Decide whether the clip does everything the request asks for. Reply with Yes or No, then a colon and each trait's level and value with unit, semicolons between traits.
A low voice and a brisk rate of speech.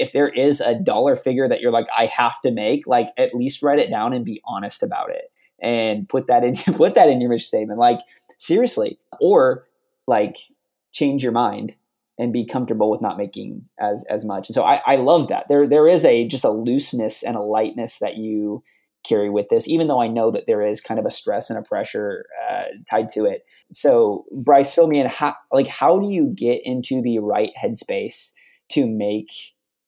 Yes: low, 130 Hz; fast, 210 wpm